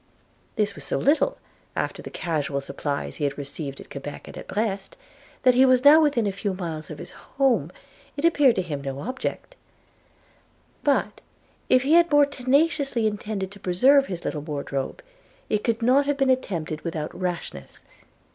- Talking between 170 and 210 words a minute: Yes, average, 175 wpm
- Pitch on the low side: No, high, 210 Hz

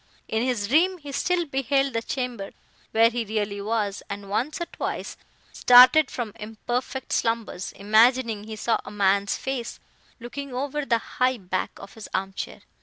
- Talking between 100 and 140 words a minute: No, average, 165 wpm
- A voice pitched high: Yes, high, 230 Hz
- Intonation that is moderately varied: Yes, average, 4.2 semitones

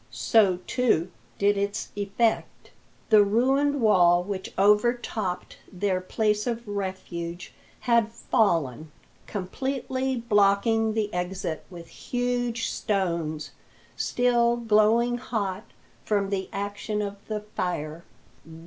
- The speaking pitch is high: Yes, high, 205 Hz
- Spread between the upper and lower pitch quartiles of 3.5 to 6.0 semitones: Yes, average, 3.8 semitones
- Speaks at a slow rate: Yes, slow, 105 wpm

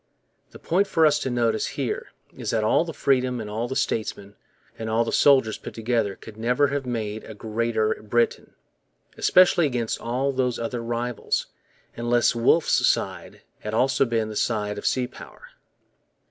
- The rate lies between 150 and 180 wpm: Yes, average, 170 wpm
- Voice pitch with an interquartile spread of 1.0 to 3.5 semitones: Yes, average, 2.8 semitones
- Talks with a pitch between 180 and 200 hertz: No, low, 120 Hz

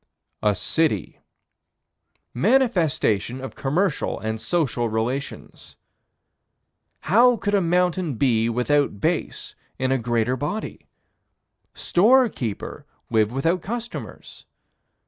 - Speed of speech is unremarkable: No, slow, 90 wpm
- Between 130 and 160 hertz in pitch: Yes, medium, 140 Hz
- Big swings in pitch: Yes, wide, 7.7 semitones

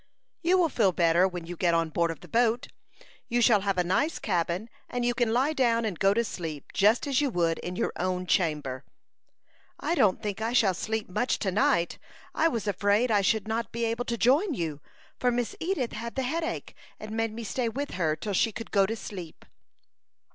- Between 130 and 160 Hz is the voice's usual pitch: No, high, 220 Hz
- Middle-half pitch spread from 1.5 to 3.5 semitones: No, average, 5.0 semitones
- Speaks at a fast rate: Yes, fast, 215 wpm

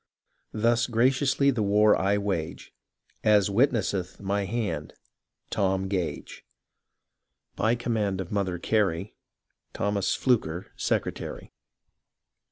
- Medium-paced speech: No, slow, 105 wpm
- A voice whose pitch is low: Yes, low, 100 Hz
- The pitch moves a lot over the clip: No, average, 3.3 semitones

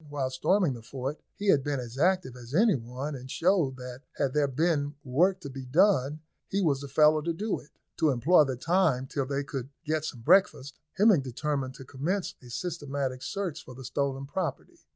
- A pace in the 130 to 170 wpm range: No, average, 200 wpm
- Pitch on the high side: No, medium, 140 Hz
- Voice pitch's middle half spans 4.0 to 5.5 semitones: Yes, average, 4.3 semitones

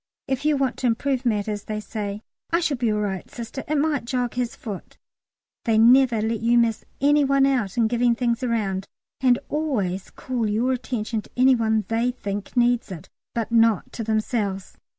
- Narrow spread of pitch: No, average, 3.2 semitones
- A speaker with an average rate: Yes, average, 190 wpm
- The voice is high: Yes, high, 235 Hz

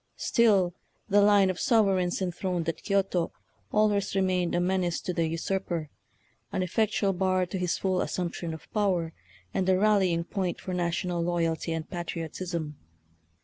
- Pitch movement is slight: Yes, narrow, 2.2 semitones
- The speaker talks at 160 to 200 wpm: No, average, 150 wpm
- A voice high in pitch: No, medium, 180 Hz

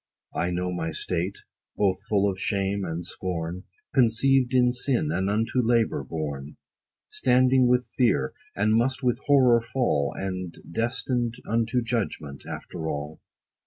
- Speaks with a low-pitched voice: Yes, low, 110 Hz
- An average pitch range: No, wide, 5.7 semitones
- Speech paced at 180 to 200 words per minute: No, slow, 135 wpm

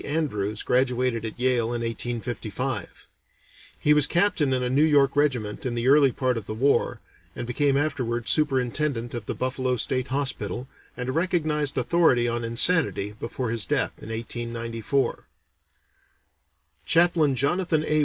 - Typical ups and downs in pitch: Yes, average, 3.8 semitones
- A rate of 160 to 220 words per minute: No, average, 145 wpm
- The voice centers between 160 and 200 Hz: No, low, 130 Hz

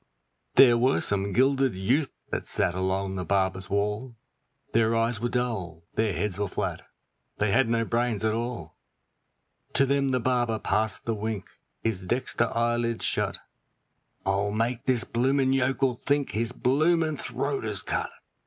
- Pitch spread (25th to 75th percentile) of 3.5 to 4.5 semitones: Yes, average, 3.9 semitones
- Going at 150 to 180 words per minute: Yes, average, 155 wpm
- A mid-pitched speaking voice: No, low, 115 Hz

